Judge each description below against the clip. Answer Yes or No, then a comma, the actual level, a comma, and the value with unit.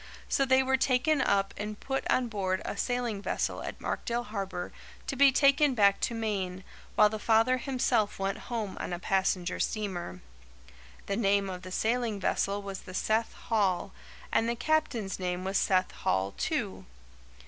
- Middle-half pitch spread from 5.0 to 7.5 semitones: No, average, 4.2 semitones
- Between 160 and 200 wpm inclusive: Yes, average, 170 wpm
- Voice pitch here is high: Yes, high, 210 Hz